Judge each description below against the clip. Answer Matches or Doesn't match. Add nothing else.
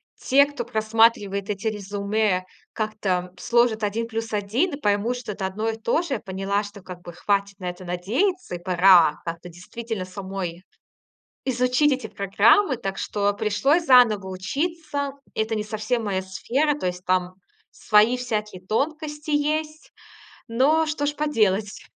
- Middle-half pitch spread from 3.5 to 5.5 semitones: Matches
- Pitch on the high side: Matches